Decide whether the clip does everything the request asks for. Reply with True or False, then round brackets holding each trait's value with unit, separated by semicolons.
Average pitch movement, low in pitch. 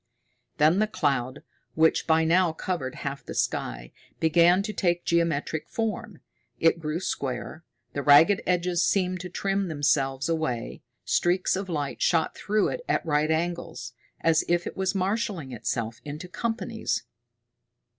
False (4.0 semitones; 165 Hz)